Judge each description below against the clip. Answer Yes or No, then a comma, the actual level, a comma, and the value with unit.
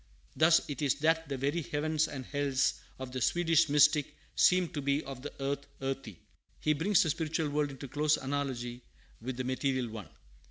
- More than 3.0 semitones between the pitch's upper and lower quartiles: No, average, 2.7 semitones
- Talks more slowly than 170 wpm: No, average, 185 wpm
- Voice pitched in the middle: Yes, medium, 145 Hz